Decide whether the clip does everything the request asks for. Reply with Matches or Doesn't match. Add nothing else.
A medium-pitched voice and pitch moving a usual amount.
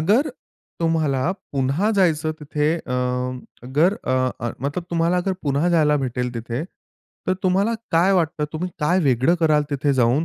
Matches